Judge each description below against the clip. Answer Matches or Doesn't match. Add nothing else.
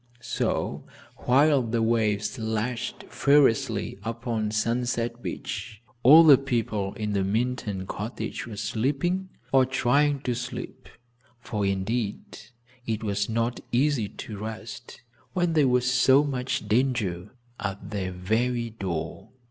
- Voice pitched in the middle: Doesn't match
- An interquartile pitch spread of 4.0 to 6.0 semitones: Doesn't match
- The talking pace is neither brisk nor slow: Doesn't match